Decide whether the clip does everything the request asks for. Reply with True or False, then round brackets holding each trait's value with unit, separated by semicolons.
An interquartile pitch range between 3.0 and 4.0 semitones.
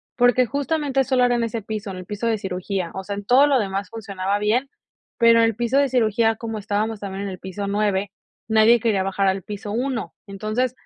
True (3.3 semitones)